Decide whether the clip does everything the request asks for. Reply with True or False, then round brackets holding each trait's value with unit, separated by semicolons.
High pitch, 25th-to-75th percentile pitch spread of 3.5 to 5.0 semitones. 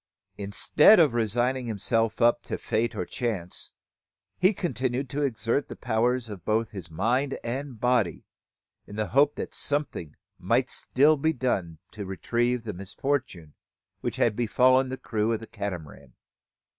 False (120 Hz; 3.8 semitones)